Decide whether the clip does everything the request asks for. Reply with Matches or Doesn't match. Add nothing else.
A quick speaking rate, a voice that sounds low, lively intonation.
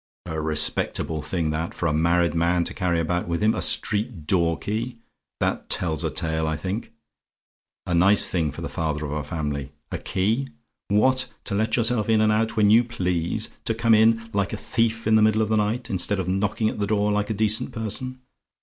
Doesn't match